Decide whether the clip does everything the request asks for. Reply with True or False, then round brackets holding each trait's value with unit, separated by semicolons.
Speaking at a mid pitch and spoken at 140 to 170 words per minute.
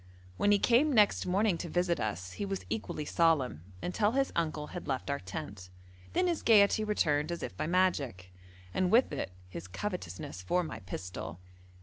False (160 Hz; 180 wpm)